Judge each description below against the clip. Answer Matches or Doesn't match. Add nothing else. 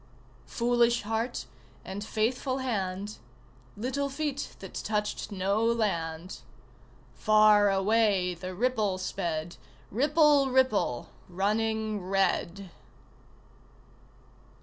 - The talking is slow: Matches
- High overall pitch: Matches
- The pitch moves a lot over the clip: Doesn't match